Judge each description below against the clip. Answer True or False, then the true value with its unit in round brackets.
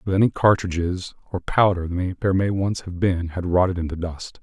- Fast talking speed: False (190 wpm)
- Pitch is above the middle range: False (90 Hz)